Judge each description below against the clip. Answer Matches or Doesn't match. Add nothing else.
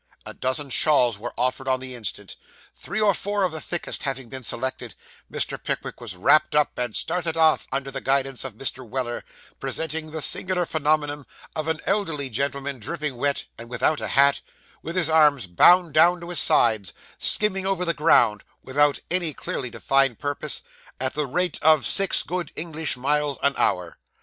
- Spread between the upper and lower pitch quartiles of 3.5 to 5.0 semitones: Matches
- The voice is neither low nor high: Matches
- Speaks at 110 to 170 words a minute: Doesn't match